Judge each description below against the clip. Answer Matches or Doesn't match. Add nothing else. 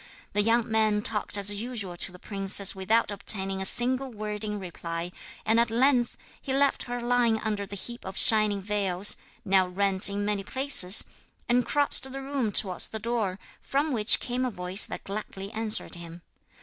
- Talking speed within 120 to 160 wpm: Doesn't match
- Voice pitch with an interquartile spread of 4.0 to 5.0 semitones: Doesn't match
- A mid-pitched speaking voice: Doesn't match